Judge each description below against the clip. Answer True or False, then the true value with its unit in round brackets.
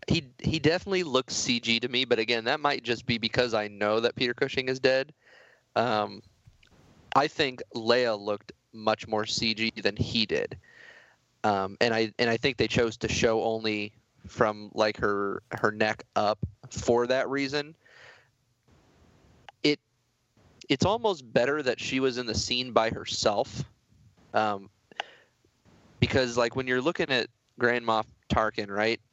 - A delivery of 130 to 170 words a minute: True (150 wpm)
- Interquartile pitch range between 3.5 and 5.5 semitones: False (2.8 semitones)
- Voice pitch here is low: True (115 Hz)